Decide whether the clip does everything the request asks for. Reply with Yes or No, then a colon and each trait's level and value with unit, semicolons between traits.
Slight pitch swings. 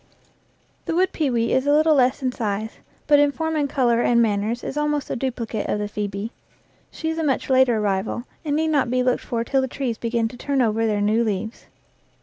No: average, 4.4 semitones